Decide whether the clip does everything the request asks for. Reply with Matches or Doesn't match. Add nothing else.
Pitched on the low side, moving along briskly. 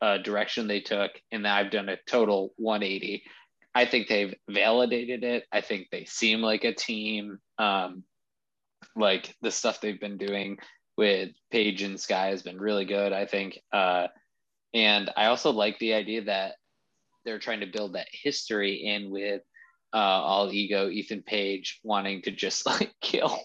Doesn't match